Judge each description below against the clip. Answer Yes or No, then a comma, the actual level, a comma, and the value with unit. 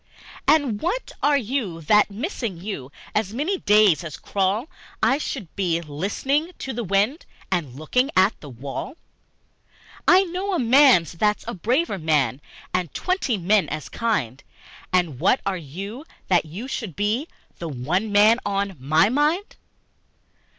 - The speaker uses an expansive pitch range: Yes, wide, 7.8 semitones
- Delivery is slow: No, average, 150 wpm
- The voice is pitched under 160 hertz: No, high, 205 Hz